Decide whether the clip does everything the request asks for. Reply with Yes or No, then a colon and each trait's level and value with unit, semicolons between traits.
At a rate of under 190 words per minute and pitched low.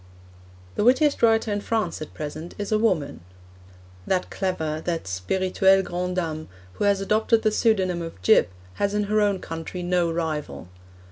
No: average, 160 wpm; medium, 185 Hz